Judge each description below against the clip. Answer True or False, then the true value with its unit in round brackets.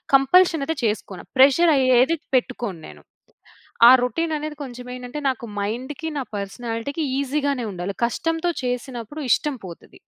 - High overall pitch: True (260 Hz)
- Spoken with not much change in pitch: False (4.1 semitones)